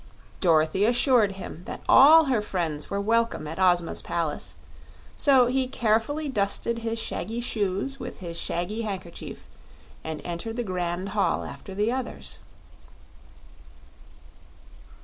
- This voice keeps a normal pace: No, slow, 125 wpm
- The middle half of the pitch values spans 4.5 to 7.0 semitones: Yes, average, 5.2 semitones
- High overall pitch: Yes, high, 205 Hz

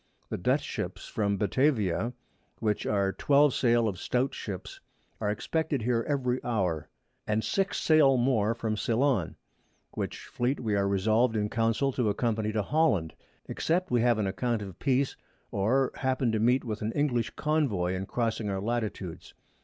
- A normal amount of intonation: Yes, average, 4.0 semitones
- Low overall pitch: Yes, low, 115 Hz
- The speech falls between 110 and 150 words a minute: No, average, 160 wpm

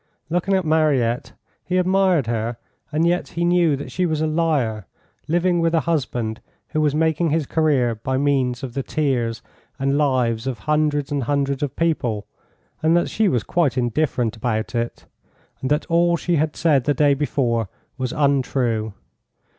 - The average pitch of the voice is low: No, medium, 145 Hz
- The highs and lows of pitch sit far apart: No, average, 4.7 semitones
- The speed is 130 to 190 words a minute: Yes, average, 170 wpm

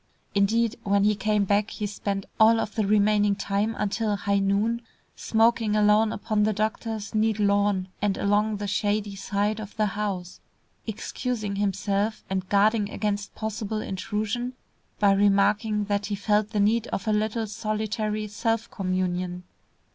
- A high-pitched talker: Yes, high, 210 Hz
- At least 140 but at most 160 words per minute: Yes, average, 150 wpm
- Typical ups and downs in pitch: No, narrow, 1.3 semitones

